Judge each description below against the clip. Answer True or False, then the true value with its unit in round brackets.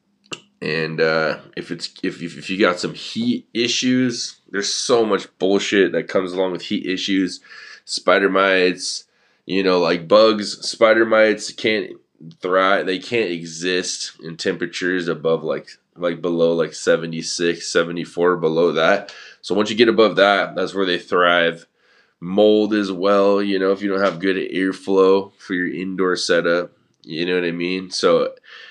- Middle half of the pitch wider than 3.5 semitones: False (2.4 semitones)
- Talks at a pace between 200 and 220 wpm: False (160 wpm)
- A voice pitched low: True (95 Hz)